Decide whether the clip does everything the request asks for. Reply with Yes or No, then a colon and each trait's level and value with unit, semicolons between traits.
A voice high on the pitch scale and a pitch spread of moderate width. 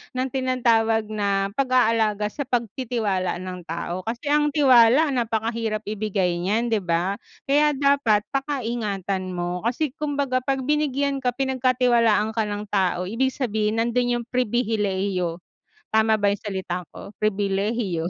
Yes: high, 225 Hz; average, 4.3 semitones